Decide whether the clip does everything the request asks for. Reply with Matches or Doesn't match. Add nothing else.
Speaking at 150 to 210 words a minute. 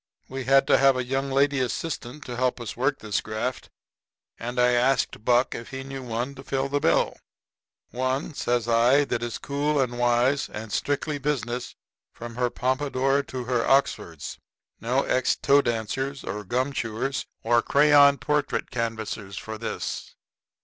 Matches